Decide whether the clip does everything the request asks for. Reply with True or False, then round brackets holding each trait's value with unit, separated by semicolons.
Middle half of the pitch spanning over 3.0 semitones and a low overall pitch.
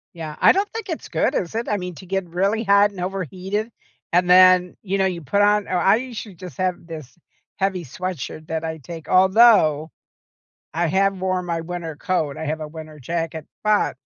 False (3.4 semitones; 180 Hz)